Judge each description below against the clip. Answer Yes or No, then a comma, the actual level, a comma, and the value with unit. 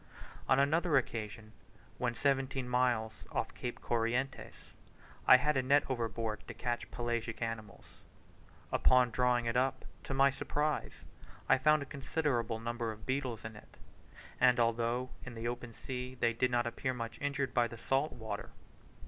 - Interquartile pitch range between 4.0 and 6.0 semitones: No, narrow, 2.4 semitones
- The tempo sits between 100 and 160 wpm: Yes, average, 155 wpm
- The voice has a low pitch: Yes, low, 125 Hz